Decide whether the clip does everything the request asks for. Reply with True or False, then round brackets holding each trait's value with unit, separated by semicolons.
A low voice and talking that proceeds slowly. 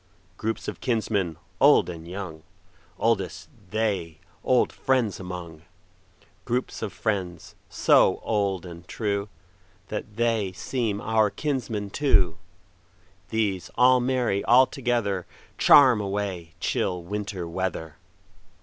True (100 Hz; 95 wpm)